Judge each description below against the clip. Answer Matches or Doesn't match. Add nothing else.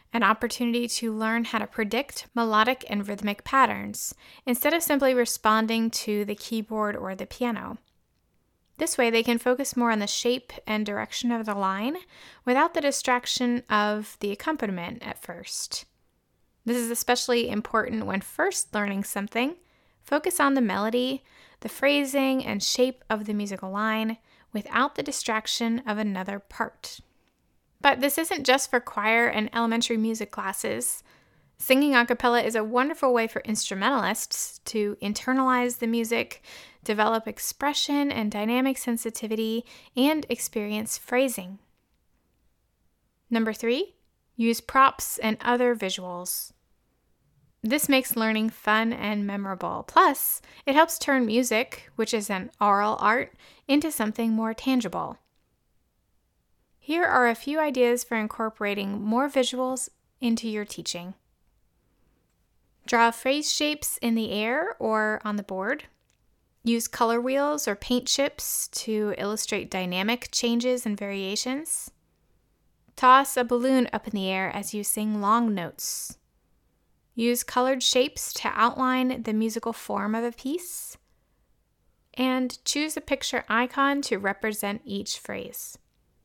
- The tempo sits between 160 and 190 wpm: Doesn't match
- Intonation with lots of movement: Doesn't match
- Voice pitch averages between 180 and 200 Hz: Doesn't match